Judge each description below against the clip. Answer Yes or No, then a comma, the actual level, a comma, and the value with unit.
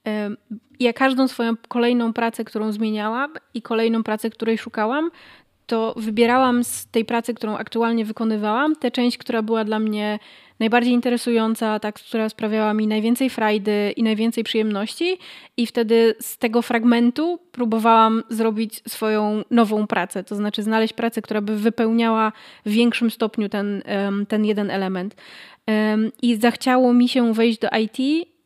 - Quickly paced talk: No, average, 145 wpm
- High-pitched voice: Yes, high, 225 Hz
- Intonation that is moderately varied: No, narrow, 1.8 semitones